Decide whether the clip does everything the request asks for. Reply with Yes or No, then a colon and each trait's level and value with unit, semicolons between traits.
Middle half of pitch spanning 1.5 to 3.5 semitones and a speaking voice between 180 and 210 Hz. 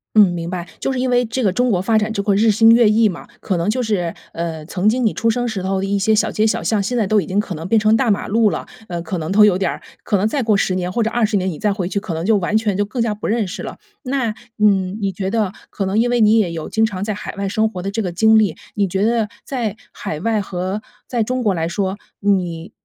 Yes: average, 3.0 semitones; high, 205 Hz